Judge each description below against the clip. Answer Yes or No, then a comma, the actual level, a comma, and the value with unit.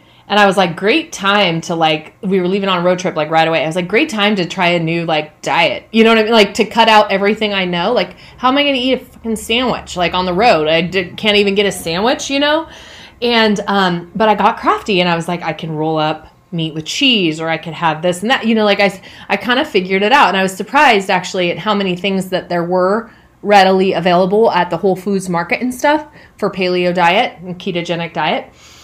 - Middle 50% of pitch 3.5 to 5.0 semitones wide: Yes, average, 4.0 semitones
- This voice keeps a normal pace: No, fast, 260 wpm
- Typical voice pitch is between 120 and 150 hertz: No, high, 190 Hz